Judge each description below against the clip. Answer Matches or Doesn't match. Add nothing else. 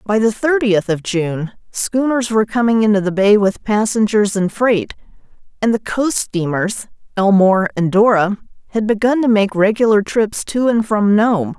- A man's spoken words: Doesn't match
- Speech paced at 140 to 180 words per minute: Matches